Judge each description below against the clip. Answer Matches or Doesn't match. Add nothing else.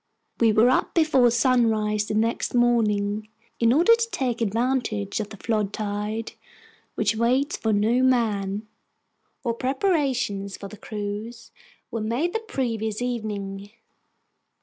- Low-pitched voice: Doesn't match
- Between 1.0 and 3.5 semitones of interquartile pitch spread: Matches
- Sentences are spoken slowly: Matches